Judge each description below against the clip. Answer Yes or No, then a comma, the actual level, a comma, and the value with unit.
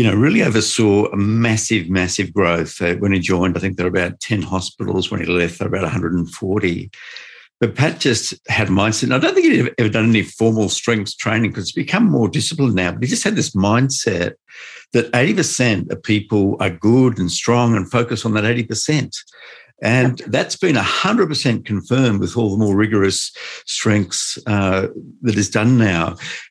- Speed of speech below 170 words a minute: No, average, 185 wpm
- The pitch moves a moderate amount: Yes, average, 3.9 semitones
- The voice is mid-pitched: No, low, 110 Hz